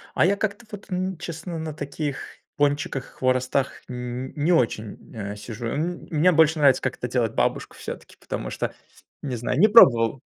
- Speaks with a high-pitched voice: No, medium, 145 Hz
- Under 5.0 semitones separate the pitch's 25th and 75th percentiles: No, average, 5.3 semitones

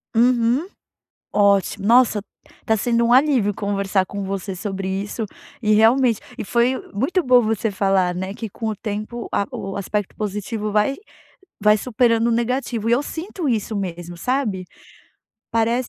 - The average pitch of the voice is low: No, high, 215 Hz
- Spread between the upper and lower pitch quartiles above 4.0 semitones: No, average, 3.3 semitones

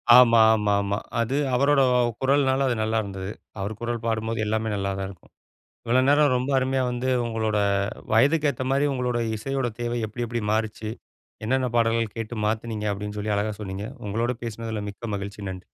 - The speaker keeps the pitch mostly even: No, average, 3.2 semitones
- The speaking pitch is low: Yes, low, 115 Hz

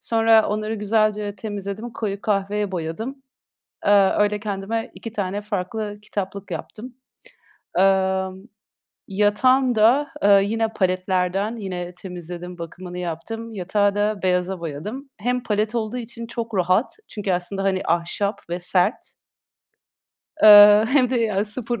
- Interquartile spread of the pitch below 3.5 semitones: Yes, average, 2.9 semitones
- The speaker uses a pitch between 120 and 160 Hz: No, high, 205 Hz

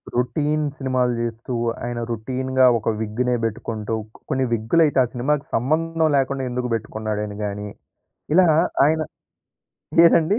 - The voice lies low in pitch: Yes, low, 125 Hz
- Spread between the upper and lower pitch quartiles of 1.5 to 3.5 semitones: No, average, 4.6 semitones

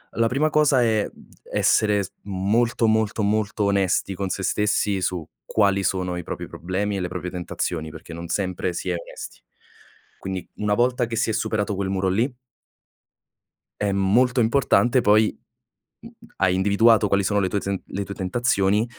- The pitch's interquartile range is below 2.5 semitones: No, average, 2.9 semitones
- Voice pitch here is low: Yes, low, 100 Hz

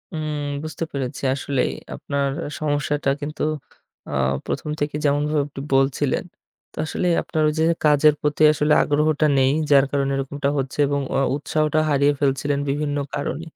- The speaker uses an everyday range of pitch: No, narrow, 1.5 semitones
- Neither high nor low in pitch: Yes, medium, 145 Hz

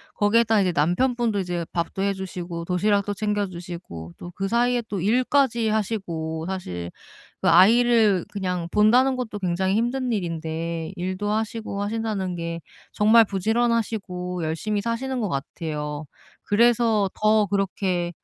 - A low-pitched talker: No, high, 200 Hz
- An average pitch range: Yes, average, 4.2 semitones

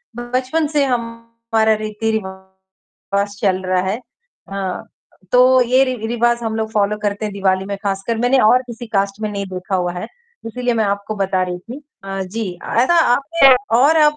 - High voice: Yes, high, 220 Hz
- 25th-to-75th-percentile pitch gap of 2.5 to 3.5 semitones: No, average, 3.9 semitones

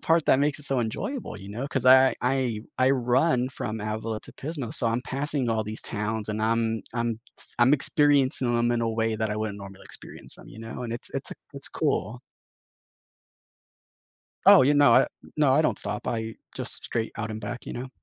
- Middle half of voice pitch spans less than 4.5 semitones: Yes, average, 3.2 semitones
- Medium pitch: No, low, 120 Hz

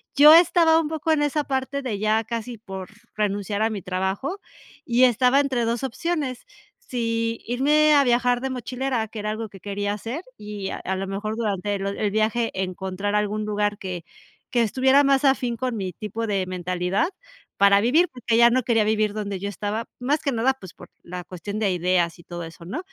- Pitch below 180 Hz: No, high, 220 Hz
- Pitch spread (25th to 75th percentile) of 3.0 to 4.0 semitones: No, average, 4.5 semitones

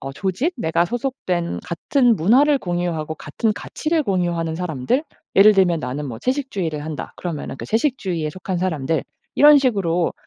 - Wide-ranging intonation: Yes, wide, 7.1 semitones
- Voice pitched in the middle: Yes, medium, 180 Hz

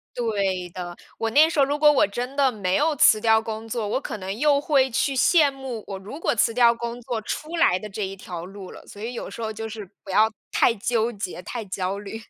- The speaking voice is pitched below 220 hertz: No, high, 225 Hz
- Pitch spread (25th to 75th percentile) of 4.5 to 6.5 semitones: Yes, average, 4.8 semitones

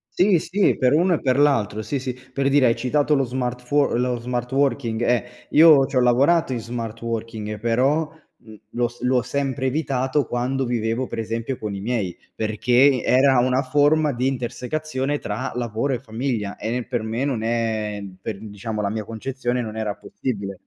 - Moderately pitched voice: No, low, 125 Hz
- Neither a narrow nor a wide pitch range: Yes, average, 3.1 semitones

